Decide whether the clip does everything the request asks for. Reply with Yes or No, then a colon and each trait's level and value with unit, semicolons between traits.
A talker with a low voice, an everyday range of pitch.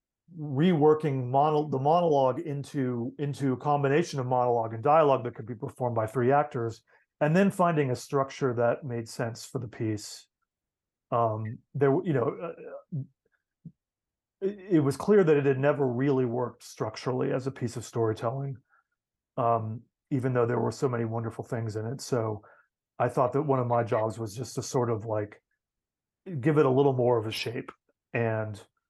Yes: low, 130 Hz; average, 3.5 semitones